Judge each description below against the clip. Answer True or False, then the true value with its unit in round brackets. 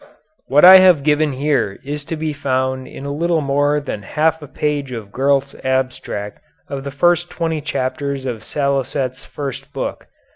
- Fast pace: False (170 wpm)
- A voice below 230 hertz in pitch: True (140 Hz)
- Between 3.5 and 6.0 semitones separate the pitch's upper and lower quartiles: False (2.4 semitones)